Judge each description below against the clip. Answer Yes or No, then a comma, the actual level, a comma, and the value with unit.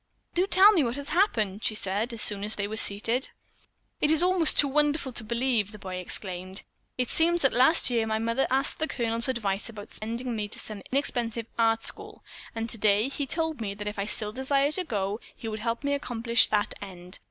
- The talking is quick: Yes, fast, 210 wpm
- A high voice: Yes, high, 230 Hz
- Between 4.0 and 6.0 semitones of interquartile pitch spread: Yes, average, 4.7 semitones